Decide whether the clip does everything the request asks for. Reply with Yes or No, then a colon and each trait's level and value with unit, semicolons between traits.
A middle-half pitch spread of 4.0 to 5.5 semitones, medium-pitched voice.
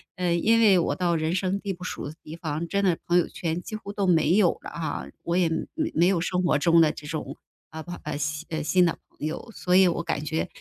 No: narrow, 2.5 semitones; medium, 170 Hz